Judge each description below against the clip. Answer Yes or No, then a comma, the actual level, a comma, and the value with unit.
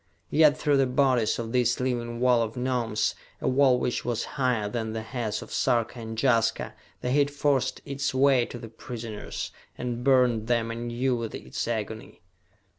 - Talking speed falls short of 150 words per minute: No, average, 175 wpm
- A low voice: Yes, low, 120 Hz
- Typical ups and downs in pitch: No, narrow, 2.3 semitones